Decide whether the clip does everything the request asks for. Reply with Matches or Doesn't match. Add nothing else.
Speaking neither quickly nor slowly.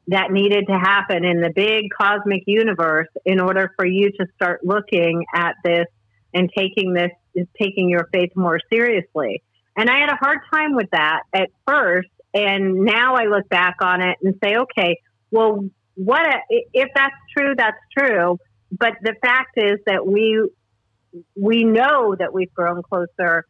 Matches